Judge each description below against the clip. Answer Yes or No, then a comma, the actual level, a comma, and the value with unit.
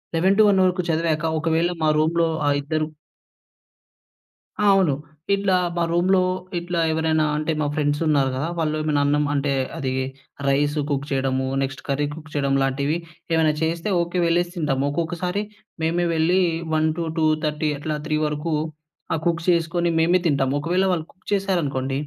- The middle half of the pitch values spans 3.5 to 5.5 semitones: No, average, 2.7 semitones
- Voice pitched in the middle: Yes, medium, 160 Hz